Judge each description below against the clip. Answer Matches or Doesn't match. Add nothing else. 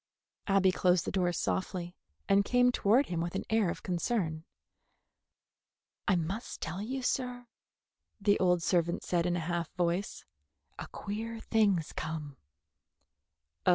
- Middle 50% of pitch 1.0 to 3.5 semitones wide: Doesn't match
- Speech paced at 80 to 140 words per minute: Matches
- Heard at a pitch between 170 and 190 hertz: Matches